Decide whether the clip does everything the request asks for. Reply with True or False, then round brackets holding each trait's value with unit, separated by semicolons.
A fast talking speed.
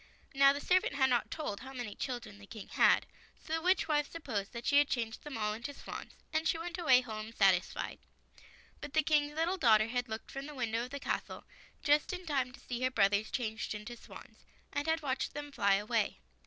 True (220 wpm)